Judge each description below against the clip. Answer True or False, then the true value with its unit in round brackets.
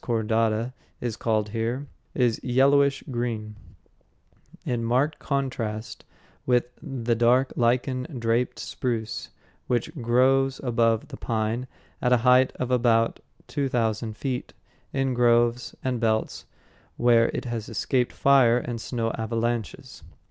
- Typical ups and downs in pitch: False (1.9 semitones)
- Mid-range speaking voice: False (120 Hz)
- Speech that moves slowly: True (120 wpm)